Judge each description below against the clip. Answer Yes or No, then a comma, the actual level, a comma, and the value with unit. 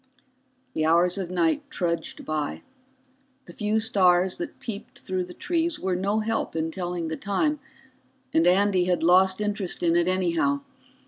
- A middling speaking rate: Yes, average, 155 wpm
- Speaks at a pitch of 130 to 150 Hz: No, medium, 185 Hz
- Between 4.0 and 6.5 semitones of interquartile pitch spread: No, average, 3.5 semitones